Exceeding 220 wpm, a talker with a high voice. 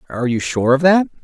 No: fast, 245 wpm; medium, 145 Hz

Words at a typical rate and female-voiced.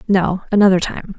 Yes: average, 150 wpm; female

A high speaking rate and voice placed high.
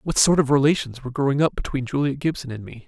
No: fast, 250 wpm; low, 135 Hz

